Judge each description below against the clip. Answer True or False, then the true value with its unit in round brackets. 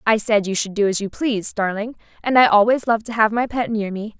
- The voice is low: False (220 Hz)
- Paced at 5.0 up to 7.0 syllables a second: True (5.8 syllables/s)